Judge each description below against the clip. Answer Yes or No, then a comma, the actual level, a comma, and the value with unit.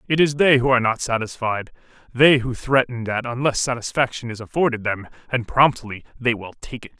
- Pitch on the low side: Yes, low, 120 Hz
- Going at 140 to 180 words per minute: No, average, 190 wpm